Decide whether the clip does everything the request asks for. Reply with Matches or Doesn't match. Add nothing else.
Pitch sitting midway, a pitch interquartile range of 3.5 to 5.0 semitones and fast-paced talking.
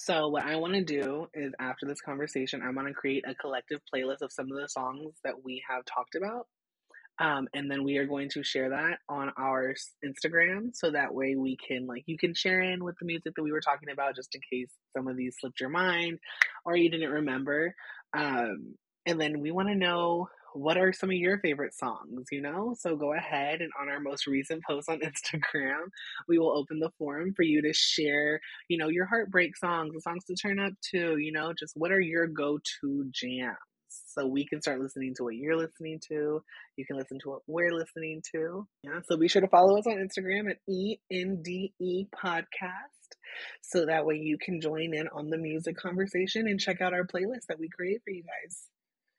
Matches